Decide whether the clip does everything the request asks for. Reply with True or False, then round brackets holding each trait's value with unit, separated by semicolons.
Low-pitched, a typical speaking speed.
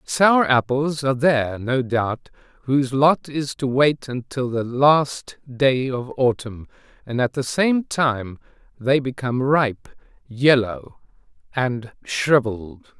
False (130 Hz; 130 wpm)